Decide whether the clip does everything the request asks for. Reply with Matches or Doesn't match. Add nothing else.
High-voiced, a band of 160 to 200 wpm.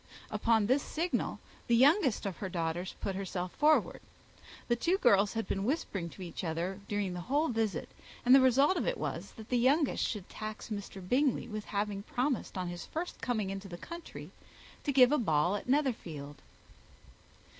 Matches